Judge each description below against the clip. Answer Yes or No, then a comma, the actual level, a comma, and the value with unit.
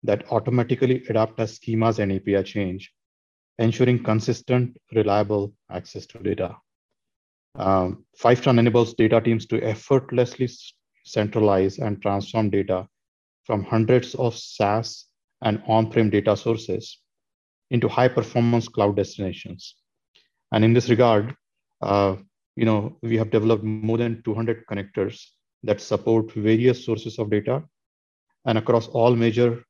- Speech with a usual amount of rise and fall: No, narrow, 2.3 semitones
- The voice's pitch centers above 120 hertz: No, low, 110 Hz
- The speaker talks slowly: Yes, slow, 125 wpm